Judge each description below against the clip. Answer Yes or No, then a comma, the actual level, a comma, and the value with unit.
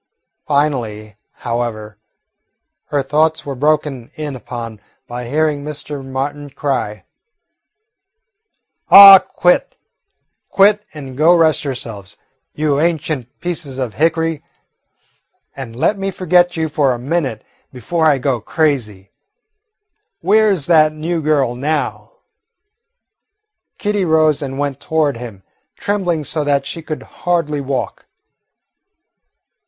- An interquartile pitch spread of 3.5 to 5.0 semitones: Yes, average, 3.9 semitones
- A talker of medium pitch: Yes, medium, 145 Hz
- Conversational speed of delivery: No, slow, 115 wpm